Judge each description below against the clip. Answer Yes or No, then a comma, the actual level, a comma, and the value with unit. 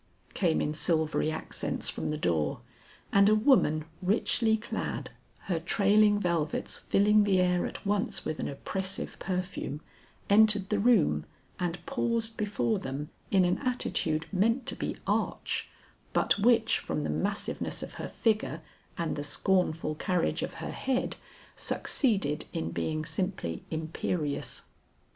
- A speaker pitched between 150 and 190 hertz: Yes, medium, 185 Hz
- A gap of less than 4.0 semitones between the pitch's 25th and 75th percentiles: No, average, 5.2 semitones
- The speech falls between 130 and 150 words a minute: Yes, average, 140 wpm